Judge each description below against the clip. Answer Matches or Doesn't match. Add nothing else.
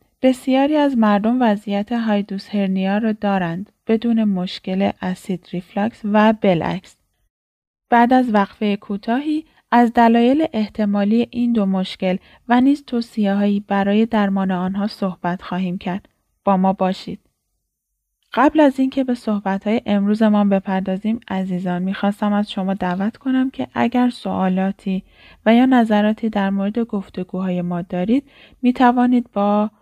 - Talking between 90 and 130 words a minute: Matches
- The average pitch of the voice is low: Doesn't match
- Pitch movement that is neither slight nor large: Matches